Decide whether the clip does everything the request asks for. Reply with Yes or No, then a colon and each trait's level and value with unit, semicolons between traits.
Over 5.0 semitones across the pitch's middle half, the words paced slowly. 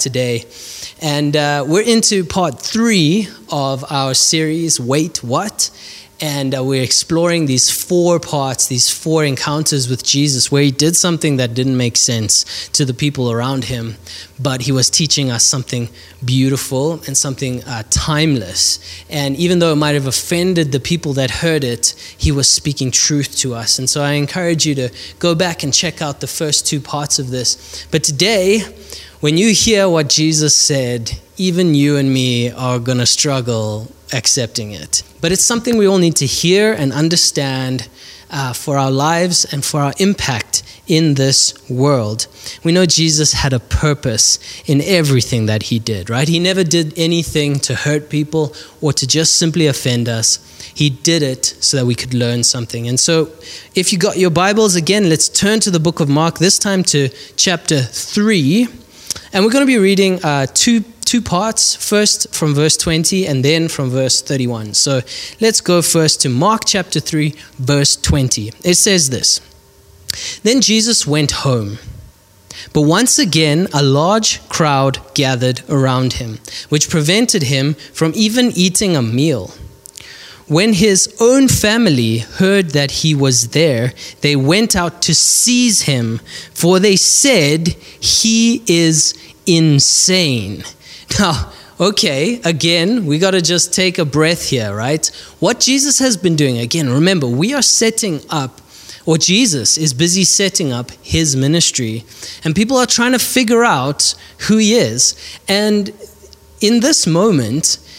No: wide, 5.4 semitones; average, 165 wpm